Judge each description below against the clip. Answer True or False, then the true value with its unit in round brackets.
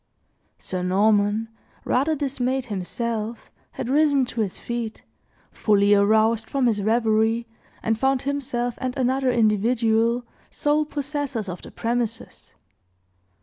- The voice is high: True (235 Hz)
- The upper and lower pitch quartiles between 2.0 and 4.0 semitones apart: True (3.3 semitones)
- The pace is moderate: False (115 wpm)